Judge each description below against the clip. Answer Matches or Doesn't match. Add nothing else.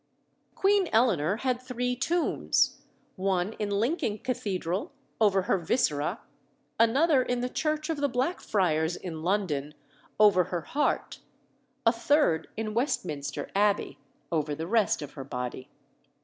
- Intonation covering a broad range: Matches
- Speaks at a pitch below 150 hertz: Doesn't match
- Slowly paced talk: Matches